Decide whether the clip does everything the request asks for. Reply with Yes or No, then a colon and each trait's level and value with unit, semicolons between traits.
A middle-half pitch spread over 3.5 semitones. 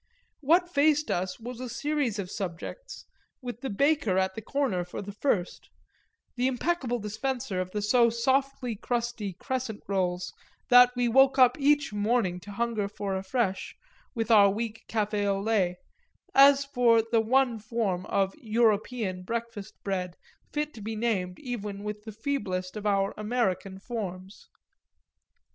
Yes: average, 4.1 semitones